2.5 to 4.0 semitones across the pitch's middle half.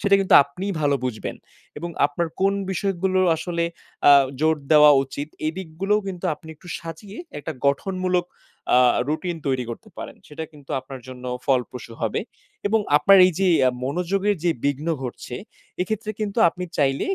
No: average, 5.1 semitones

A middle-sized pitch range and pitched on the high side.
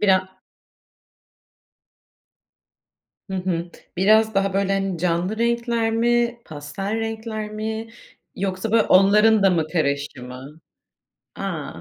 Yes: average, 3.6 semitones; high, 195 Hz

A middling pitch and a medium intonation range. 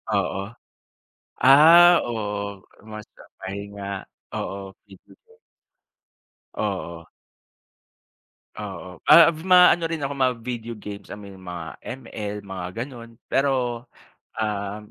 No: low, 105 Hz; average, 4.7 semitones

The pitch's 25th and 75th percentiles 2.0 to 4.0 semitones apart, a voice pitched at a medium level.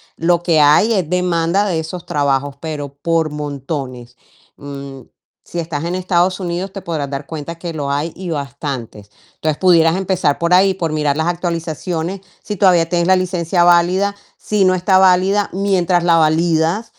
Yes: average, 3.5 semitones; medium, 170 Hz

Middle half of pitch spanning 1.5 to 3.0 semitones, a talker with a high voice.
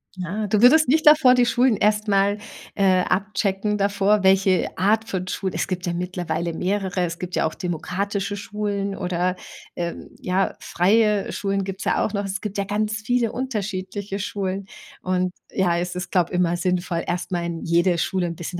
Yes: narrow, 2.4 semitones; high, 195 Hz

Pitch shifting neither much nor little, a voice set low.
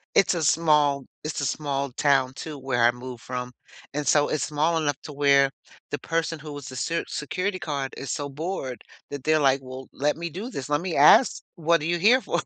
No: average, 3.1 semitones; medium, 145 Hz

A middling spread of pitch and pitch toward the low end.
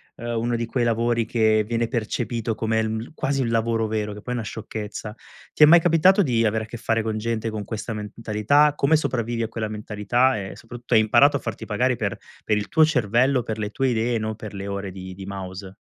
No: narrow, 2.1 semitones; low, 115 Hz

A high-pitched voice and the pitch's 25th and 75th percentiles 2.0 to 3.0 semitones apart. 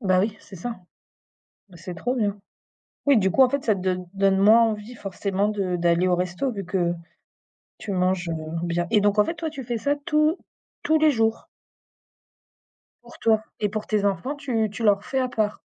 No: high, 210 Hz; average, 4.5 semitones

